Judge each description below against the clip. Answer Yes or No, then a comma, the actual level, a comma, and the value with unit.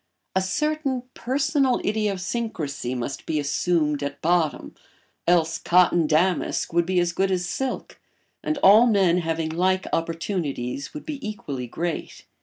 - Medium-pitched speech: Yes, medium, 180 Hz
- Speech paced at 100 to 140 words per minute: Yes, slow, 135 wpm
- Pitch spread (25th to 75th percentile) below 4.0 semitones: No, average, 5.0 semitones